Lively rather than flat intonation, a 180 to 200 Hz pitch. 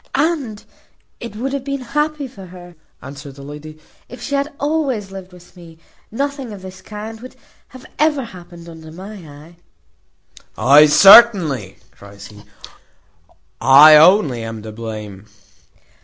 Yes: wide, 9.0 semitones; medium, 185 Hz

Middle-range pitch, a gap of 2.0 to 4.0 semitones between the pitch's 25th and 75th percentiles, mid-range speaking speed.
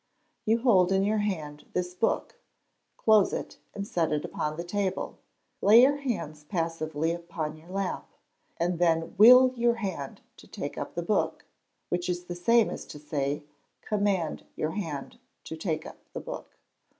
No: medium, 175 Hz; average, 4.6 semitones; average, 165 wpm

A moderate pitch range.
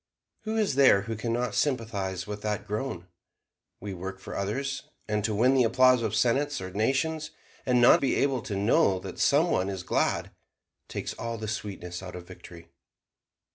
Yes: average, 4.9 semitones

